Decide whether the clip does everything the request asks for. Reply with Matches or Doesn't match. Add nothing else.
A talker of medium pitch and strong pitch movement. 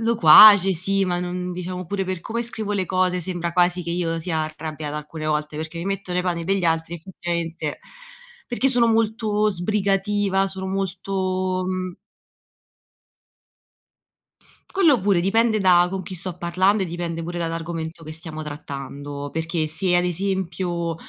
Doesn't match